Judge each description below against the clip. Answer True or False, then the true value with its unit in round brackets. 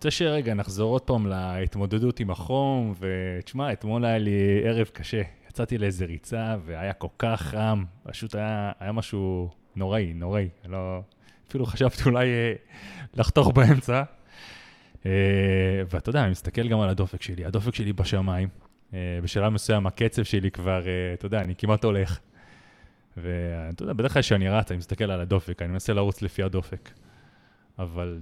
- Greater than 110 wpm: True (150 wpm)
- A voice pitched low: True (100 Hz)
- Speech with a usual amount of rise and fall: True (3.3 semitones)